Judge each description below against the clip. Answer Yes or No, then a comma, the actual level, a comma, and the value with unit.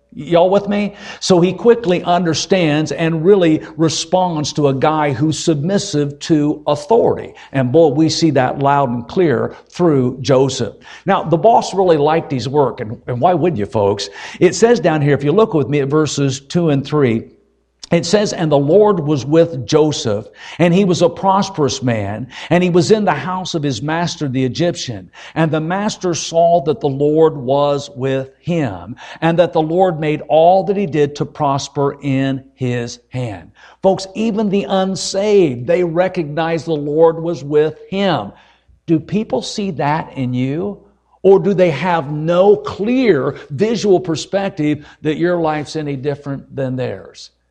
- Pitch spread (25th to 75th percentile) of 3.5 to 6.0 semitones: Yes, average, 4.3 semitones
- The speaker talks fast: No, average, 170 wpm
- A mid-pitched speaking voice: Yes, medium, 160 Hz